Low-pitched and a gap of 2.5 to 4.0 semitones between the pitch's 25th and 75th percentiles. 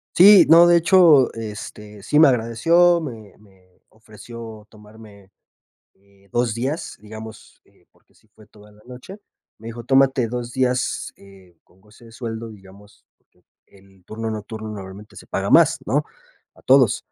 Yes: low, 110 Hz; average, 3.4 semitones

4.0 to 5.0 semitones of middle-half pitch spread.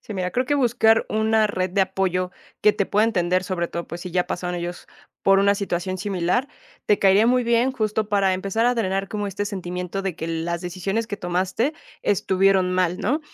No: average, 3.0 semitones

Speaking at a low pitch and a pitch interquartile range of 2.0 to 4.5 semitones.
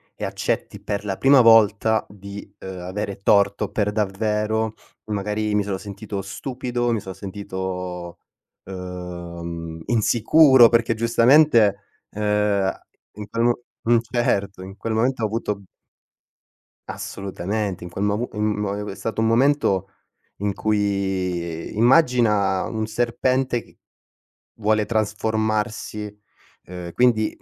Yes: low, 105 Hz; average, 2.7 semitones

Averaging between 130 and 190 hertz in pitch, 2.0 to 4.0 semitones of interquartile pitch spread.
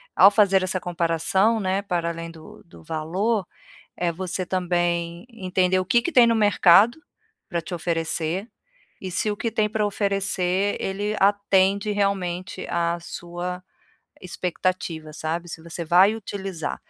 Yes: medium, 185 Hz; average, 2.8 semitones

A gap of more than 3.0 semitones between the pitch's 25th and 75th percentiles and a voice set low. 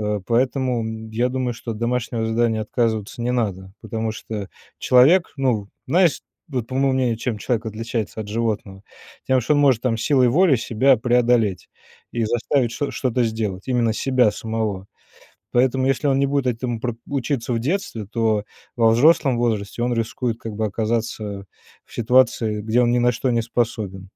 No: narrow, 2.5 semitones; low, 115 Hz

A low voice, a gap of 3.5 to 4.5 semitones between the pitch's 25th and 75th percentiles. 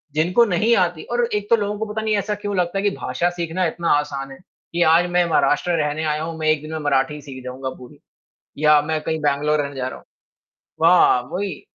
No: medium, 160 Hz; average, 3.8 semitones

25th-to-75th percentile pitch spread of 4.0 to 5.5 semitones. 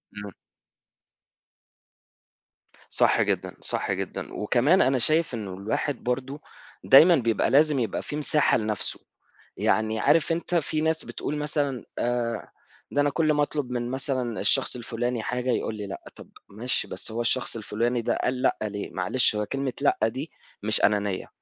Yes: average, 4.7 semitones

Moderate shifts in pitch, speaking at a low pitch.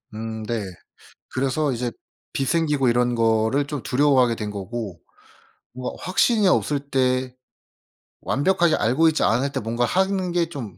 Yes: average, 4.4 semitones; low, 130 Hz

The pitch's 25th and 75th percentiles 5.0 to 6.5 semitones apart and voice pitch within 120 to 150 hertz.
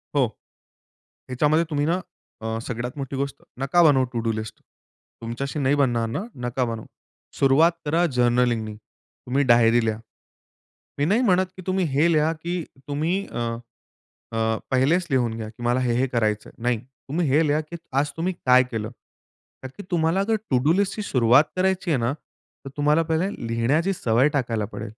Yes: wide, 5.4 semitones; low, 135 Hz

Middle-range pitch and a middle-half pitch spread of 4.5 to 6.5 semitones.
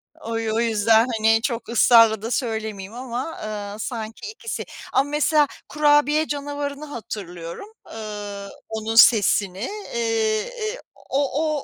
No: high, 230 Hz; average, 4.9 semitones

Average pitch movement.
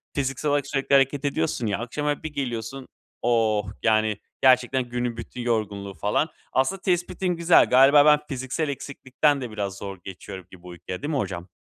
Yes: average, 5.0 semitones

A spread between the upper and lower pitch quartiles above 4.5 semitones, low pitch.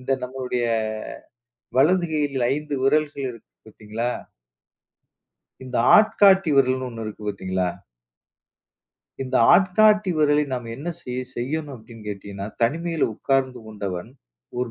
Yes: average, 4.9 semitones; low, 130 Hz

